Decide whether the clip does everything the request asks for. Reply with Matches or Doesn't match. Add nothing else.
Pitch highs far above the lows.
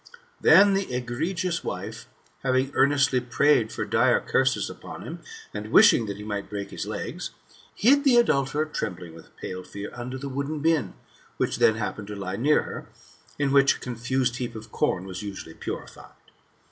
Matches